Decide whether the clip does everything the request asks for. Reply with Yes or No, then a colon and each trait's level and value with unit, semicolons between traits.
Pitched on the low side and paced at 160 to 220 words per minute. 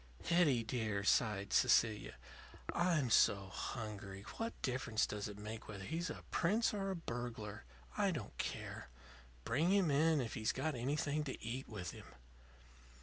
No: low, 120 Hz; average, 150 wpm